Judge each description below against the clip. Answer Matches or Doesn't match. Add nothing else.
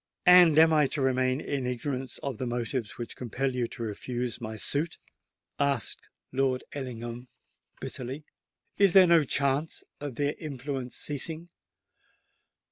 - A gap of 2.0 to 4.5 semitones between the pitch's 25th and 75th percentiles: Matches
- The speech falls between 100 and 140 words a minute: Matches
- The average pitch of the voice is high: Doesn't match